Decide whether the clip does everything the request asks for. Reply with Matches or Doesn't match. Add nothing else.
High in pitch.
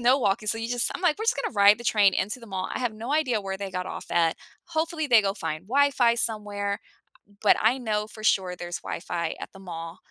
Matches